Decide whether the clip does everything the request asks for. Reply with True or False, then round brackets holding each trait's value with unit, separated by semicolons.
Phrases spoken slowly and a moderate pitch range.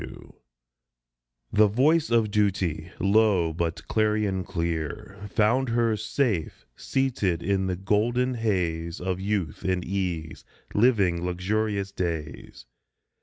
True (115 wpm; 3.7 semitones)